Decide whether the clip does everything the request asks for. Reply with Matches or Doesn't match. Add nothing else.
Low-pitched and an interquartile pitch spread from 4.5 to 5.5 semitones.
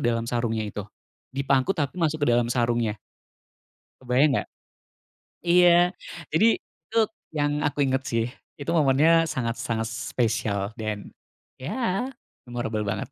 Matches